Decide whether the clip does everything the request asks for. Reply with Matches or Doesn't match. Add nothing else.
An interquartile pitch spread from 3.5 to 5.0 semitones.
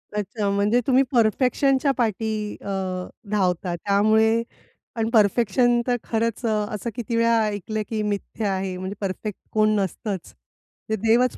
Doesn't match